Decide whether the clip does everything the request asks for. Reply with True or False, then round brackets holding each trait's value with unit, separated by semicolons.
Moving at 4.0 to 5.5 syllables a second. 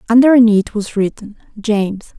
True (4.6 syllables/s)